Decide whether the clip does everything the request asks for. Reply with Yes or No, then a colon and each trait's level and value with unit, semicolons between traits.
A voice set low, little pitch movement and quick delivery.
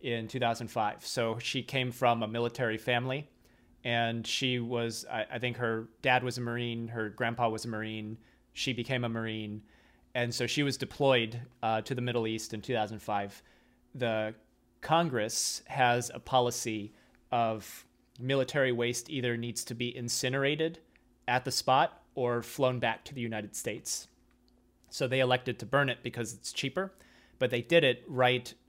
No: low, 120 Hz; narrow, 2.0 semitones; average, 165 wpm